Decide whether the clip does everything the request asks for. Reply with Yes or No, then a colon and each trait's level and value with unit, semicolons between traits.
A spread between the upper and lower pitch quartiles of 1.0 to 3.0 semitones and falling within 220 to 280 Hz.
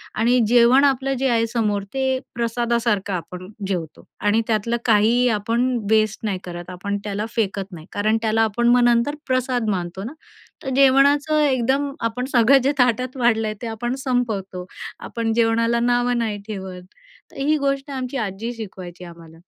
No: average, 3.5 semitones; high, 230 Hz